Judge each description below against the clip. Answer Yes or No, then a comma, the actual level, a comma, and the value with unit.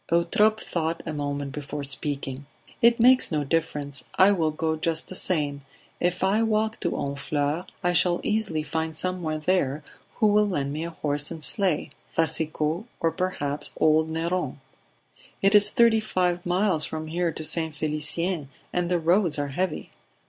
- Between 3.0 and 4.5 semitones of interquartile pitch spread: Yes, average, 3.5 semitones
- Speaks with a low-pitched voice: No, medium, 165 Hz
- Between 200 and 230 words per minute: No, average, 165 wpm